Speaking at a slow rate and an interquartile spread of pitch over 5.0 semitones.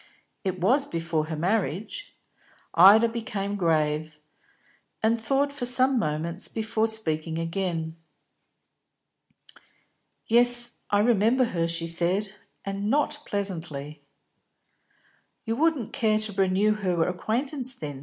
Yes: slow, 110 wpm; wide, 5.6 semitones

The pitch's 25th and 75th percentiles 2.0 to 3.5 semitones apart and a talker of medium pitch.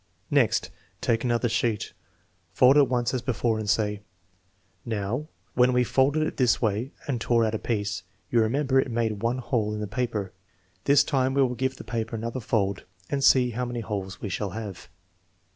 No: average, 3.0 semitones; low, 115 Hz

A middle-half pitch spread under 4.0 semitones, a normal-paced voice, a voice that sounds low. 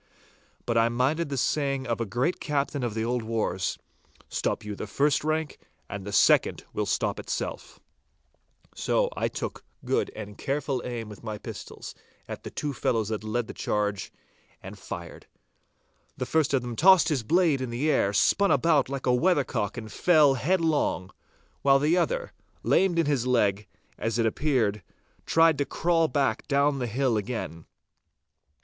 No: average, 5.1 semitones; average, 170 wpm; low, 130 Hz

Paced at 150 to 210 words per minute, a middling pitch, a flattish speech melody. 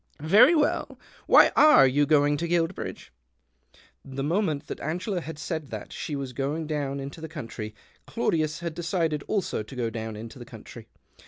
No: average, 175 wpm; medium, 150 Hz; average, 3.7 semitones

